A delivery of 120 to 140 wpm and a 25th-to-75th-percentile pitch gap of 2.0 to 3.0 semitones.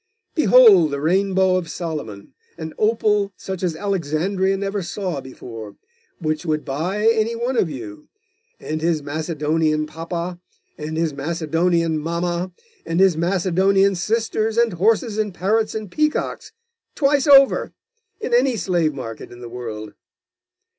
No: slow, 135 wpm; average, 4.8 semitones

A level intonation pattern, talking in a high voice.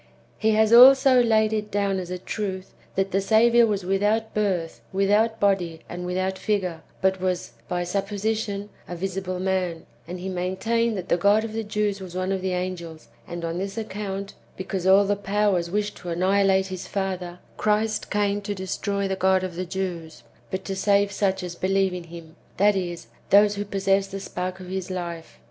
Yes: narrow, 2.1 semitones; high, 195 Hz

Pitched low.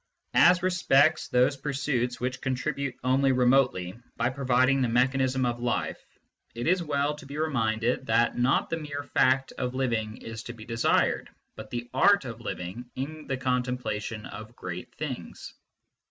Yes: low, 130 Hz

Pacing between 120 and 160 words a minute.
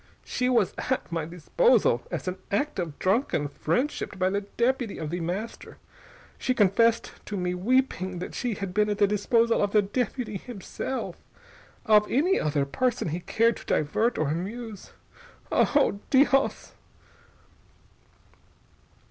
Yes: average, 140 wpm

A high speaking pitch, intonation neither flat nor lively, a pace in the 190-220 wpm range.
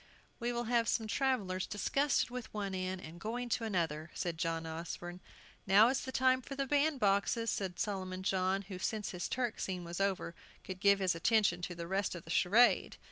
Yes: high, 195 Hz; average, 4.7 semitones; average, 195 wpm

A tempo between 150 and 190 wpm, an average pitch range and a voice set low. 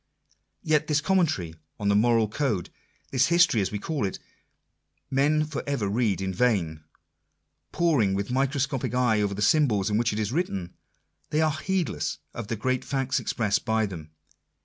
No: average, 180 wpm; wide, 6.3 semitones; low, 120 Hz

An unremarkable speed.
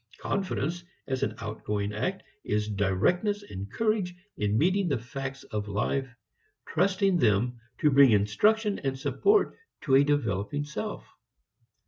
No: slow, 130 wpm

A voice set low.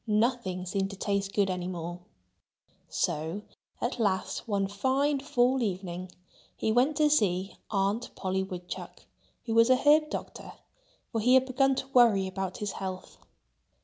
No: high, 205 Hz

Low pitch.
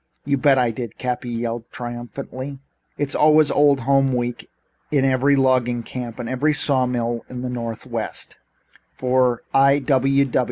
Yes: low, 125 Hz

